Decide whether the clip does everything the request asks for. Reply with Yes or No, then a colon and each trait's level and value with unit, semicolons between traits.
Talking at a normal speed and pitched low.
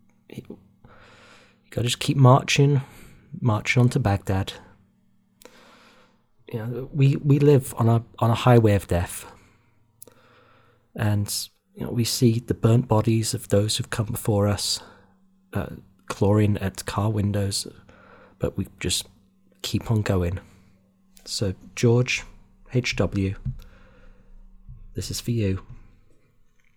No: slow, 120 wpm; low, 110 Hz